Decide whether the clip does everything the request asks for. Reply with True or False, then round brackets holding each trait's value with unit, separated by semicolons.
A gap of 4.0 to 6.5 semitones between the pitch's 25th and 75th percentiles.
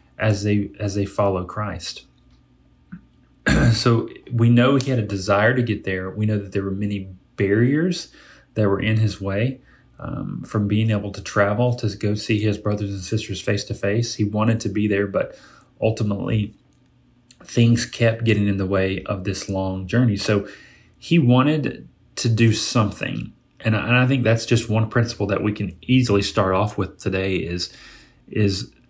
False (2.9 semitones)